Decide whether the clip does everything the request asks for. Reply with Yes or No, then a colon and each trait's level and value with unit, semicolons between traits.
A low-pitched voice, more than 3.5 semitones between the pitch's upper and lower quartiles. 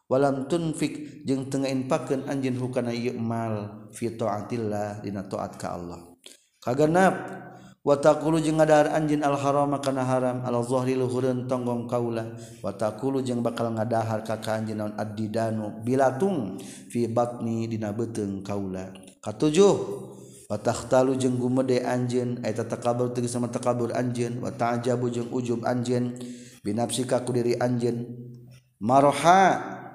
No: low, 120 Hz; narrow, 2.5 semitones